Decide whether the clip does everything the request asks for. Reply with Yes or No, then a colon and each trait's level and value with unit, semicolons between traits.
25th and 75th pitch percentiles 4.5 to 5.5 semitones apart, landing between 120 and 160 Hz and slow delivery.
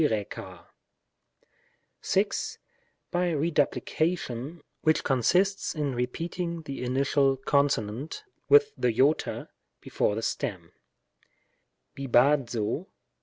Yes: average, 4.9 semitones; medium, 140 Hz; slow, 75 wpm